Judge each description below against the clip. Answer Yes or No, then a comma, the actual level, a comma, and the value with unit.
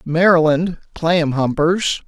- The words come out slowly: Yes, slow, 85 wpm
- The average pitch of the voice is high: No, medium, 165 Hz